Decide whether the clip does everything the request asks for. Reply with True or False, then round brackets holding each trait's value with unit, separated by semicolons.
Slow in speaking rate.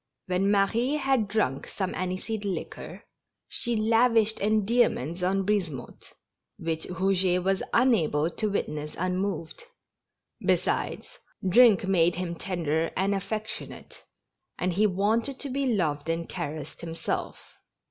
True (115 wpm)